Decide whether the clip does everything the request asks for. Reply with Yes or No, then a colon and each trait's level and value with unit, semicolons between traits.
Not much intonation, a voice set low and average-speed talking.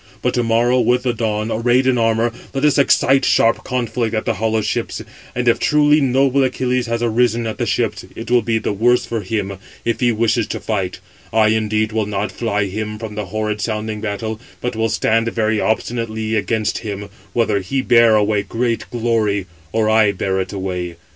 Yes: narrow, 2.1 semitones; low, 110 Hz; average, 195 wpm